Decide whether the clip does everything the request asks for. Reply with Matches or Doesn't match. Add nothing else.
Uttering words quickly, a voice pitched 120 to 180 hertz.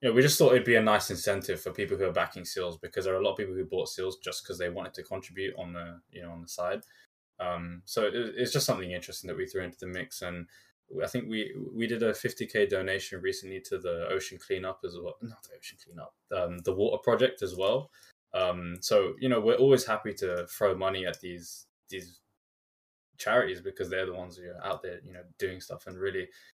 Matches